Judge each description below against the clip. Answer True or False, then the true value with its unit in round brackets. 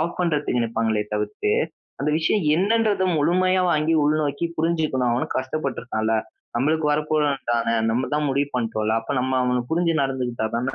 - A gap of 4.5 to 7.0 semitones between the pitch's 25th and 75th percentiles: True (4.8 semitones)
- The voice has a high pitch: False (140 Hz)